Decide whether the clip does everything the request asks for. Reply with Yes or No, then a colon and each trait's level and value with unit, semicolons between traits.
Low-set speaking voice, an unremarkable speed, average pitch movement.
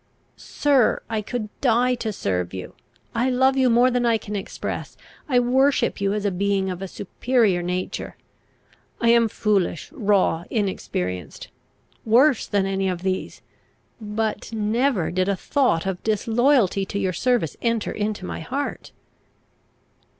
No: high, 210 Hz; average, 150 wpm; average, 4.3 semitones